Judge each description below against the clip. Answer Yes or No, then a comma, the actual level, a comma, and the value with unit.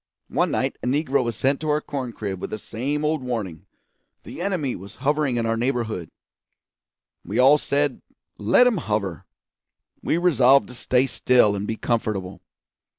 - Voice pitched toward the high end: No, low, 125 Hz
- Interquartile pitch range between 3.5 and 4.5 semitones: No, average, 5.1 semitones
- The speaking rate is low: No, average, 165 wpm